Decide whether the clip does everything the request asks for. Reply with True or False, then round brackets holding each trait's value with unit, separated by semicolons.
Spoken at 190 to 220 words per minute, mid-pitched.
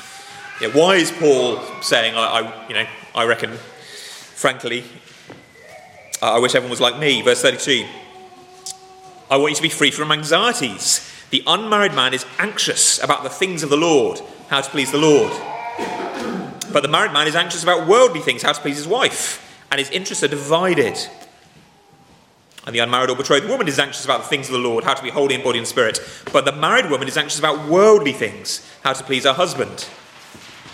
True (195 wpm; 155 Hz)